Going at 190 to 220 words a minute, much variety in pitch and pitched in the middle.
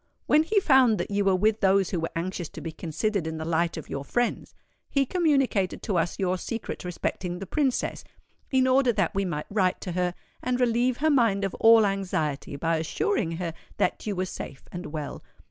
No: fast, 205 wpm; wide, 6.1 semitones; high, 195 Hz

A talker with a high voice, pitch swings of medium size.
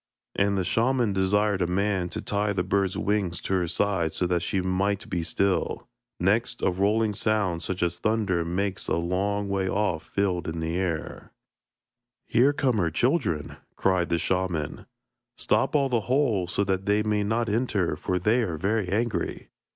No: very low, 95 Hz; average, 3.1 semitones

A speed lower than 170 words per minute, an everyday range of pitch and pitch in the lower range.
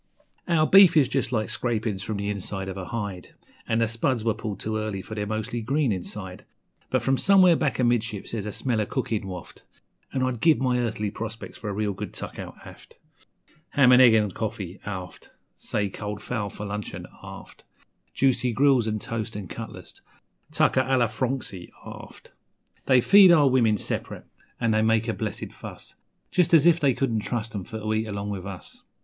No: average, 195 wpm; average, 3.8 semitones; low, 110 Hz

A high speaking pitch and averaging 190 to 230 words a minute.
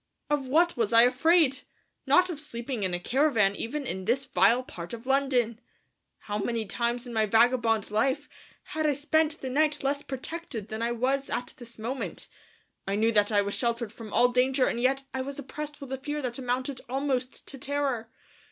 Yes: very high, 255 Hz; average, 195 wpm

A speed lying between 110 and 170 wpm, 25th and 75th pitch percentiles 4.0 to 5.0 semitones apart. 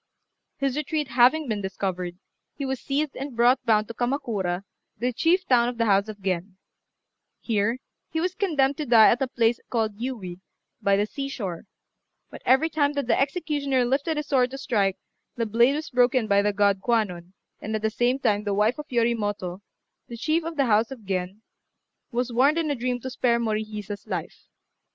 No: average, 190 wpm; average, 4.7 semitones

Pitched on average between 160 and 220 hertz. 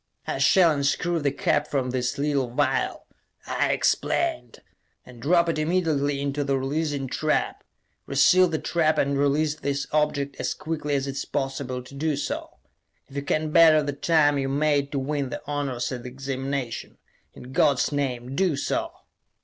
No: medium, 145 Hz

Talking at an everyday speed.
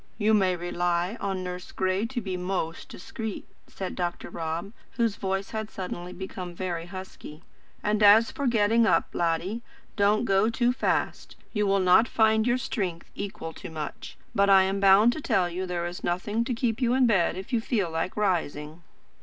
Yes: average, 185 wpm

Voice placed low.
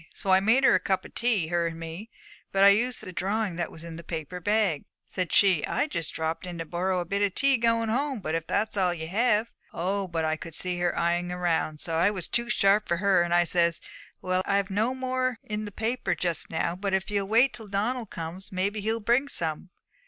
No: high, 190 Hz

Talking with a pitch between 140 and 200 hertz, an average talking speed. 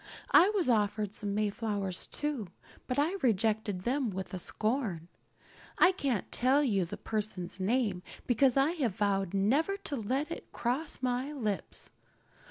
No: high, 225 Hz; average, 145 wpm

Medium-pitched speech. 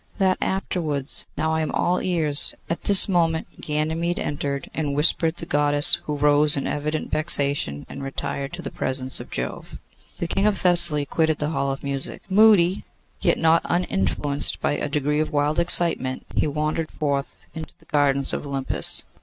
Yes: medium, 150 Hz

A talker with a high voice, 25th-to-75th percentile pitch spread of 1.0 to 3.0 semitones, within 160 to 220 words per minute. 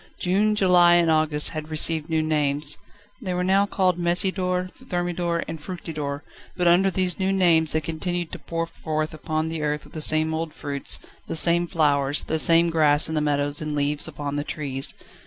No: medium, 160 Hz; average, 2.7 semitones; average, 185 wpm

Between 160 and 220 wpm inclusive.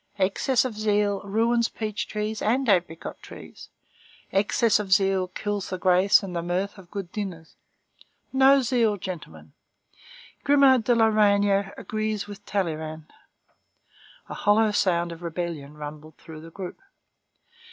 No: slow, 135 wpm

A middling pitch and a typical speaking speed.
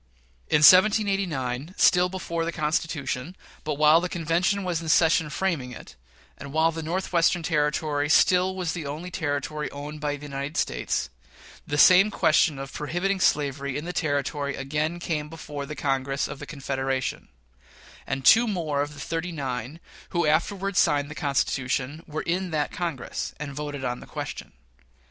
Yes: medium, 150 Hz; average, 165 wpm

